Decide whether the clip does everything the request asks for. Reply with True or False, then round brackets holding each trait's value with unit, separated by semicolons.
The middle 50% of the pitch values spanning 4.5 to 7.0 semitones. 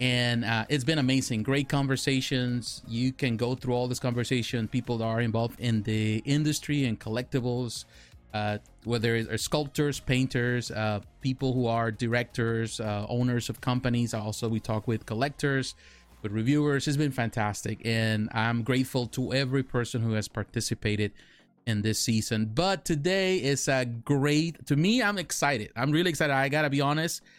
False (3.6 semitones)